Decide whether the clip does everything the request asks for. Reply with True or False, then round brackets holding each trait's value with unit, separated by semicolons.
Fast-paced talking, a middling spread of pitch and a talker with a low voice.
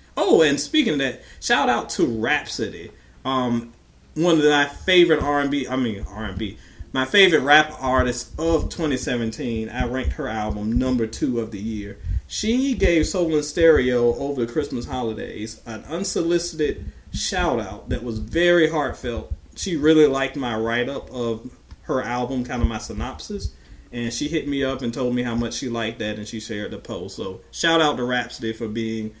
False (175 wpm; 5.0 semitones; 125 Hz)